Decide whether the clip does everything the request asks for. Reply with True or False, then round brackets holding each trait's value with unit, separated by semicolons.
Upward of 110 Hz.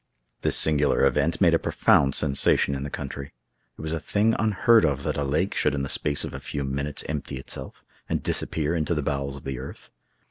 False (70 Hz)